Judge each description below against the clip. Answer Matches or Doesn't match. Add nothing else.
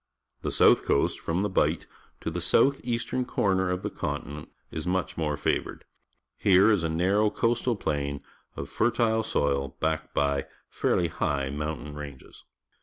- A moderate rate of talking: Matches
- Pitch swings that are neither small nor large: Doesn't match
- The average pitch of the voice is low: Matches